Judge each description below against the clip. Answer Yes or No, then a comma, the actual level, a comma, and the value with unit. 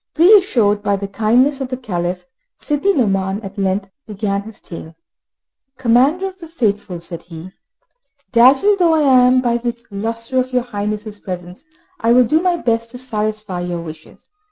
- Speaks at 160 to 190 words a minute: Yes, average, 165 wpm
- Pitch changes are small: No, average, 4.7 semitones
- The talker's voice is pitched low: No, high, 230 Hz